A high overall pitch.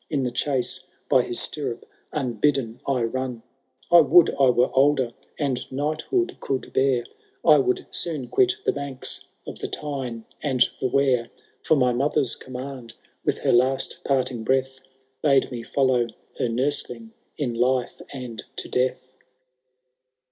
No: low, 130 Hz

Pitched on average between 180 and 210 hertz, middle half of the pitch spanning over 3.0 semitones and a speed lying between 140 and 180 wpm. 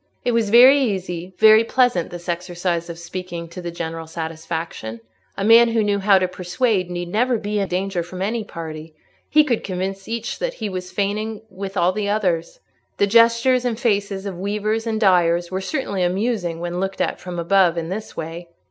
No: high, 190 Hz; average, 3.9 semitones; average, 190 wpm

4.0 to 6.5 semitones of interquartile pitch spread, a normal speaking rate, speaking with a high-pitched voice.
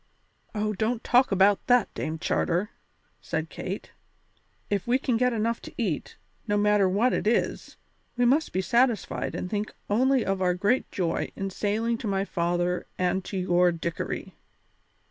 Yes: average, 4.3 semitones; average, 165 wpm; high, 205 Hz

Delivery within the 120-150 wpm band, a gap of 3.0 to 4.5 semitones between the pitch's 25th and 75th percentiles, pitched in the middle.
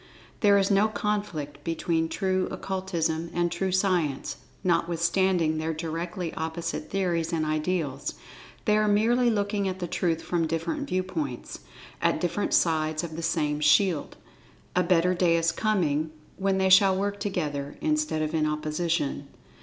Yes: average, 140 wpm; average, 3.3 semitones; medium, 170 Hz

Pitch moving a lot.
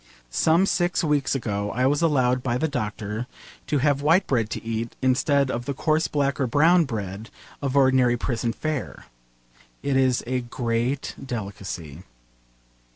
No: average, 3.8 semitones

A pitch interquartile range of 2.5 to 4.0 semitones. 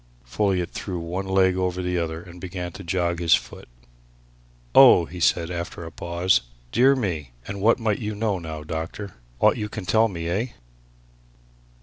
Yes: average, 3.0 semitones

